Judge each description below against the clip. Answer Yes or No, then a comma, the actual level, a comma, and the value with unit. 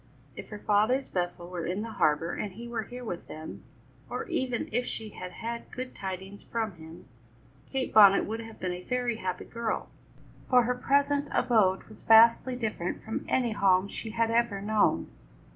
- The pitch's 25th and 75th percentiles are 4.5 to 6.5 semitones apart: No, average, 4.1 semitones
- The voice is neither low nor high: No, high, 220 Hz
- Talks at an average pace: Yes, average, 180 wpm